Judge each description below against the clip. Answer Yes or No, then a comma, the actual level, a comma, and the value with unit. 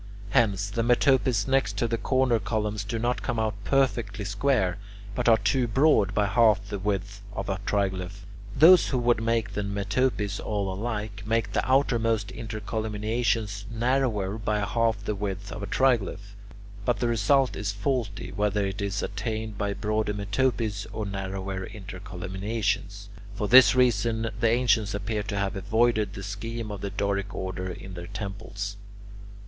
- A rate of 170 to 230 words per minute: No, average, 160 wpm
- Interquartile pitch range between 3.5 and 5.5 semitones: No, narrow, 2.5 semitones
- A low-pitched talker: Yes, low, 105 Hz